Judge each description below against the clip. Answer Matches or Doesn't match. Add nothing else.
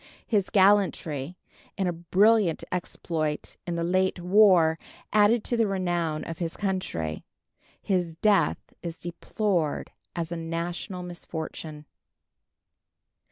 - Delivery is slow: Matches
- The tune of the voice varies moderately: Matches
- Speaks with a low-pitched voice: Doesn't match